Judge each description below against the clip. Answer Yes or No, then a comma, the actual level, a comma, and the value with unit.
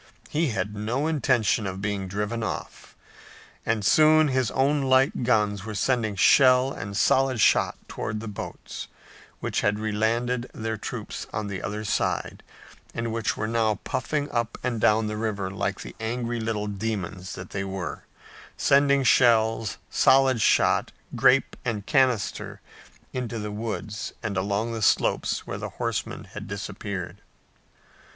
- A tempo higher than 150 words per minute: No, average, 145 wpm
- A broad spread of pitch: No, average, 3.4 semitones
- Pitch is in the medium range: No, low, 110 Hz